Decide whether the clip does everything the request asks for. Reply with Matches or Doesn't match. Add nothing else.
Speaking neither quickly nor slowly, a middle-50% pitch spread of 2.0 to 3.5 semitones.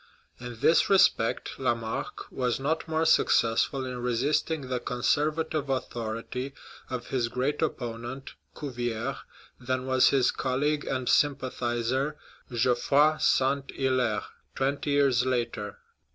Doesn't match